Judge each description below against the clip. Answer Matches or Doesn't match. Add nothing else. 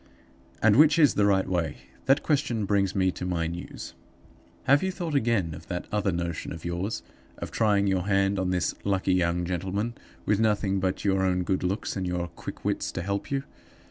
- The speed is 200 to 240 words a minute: Matches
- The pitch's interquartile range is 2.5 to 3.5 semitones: Matches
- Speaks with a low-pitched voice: Matches